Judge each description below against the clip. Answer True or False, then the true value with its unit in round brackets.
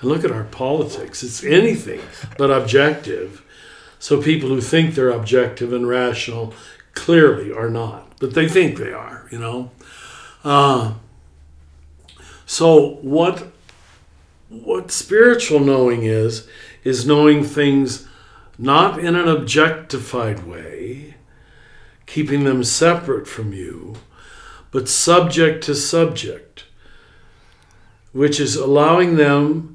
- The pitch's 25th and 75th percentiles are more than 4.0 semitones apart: True (4.9 semitones)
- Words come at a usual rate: False (110 wpm)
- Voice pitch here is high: False (135 Hz)